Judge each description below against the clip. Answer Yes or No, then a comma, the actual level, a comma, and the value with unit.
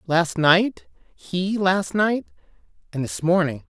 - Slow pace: Yes, slow, 110 wpm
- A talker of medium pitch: Yes, medium, 180 Hz